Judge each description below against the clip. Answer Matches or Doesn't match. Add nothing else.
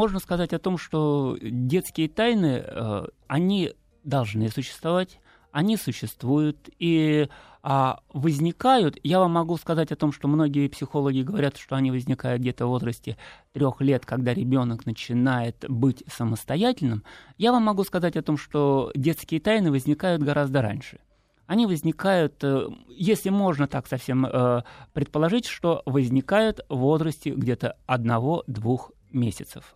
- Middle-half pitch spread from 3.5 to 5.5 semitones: Matches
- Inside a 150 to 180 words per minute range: Doesn't match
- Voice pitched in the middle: Matches